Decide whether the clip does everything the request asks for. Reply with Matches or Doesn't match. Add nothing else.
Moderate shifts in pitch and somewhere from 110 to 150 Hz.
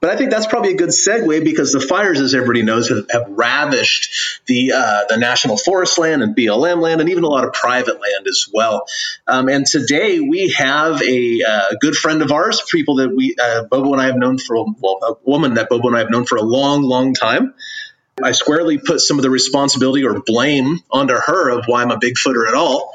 Doesn't match